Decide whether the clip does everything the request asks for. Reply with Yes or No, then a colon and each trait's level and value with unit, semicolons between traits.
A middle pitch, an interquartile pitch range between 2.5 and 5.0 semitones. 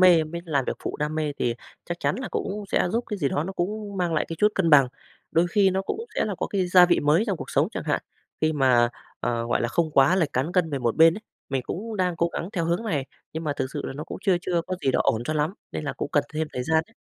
Yes: medium, 165 Hz; average, 4.2 semitones